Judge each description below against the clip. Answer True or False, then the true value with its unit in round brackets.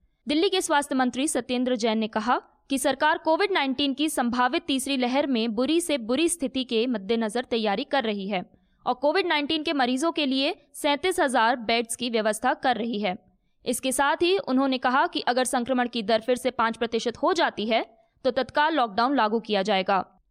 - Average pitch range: True (3.9 semitones)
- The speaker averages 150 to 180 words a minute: False (190 wpm)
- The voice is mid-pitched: False (260 Hz)